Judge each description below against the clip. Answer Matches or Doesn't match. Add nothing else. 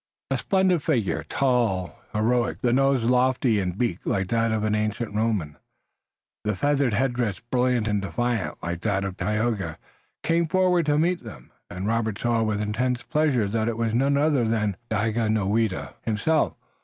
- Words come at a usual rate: Matches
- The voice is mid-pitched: Doesn't match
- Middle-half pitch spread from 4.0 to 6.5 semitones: Doesn't match